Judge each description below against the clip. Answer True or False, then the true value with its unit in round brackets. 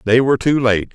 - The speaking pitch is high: False (125 Hz)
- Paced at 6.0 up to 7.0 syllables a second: True (6.2 syllables/s)